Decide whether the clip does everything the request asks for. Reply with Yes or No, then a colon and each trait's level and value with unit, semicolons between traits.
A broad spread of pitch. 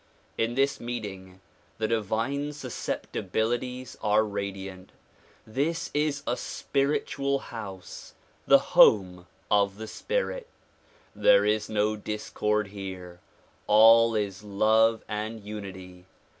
No: average, 3.3 semitones